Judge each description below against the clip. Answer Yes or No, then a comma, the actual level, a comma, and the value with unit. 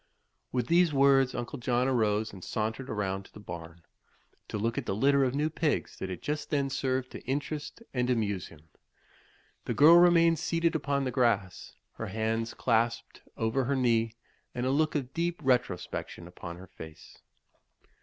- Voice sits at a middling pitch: No, low, 125 Hz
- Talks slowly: No, average, 170 wpm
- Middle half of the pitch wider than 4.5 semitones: Yes, average, 4.9 semitones